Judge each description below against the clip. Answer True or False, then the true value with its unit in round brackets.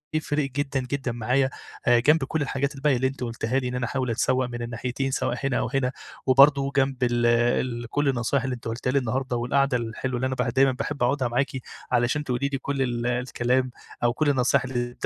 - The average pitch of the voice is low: True (130 Hz)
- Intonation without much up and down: True (2.1 semitones)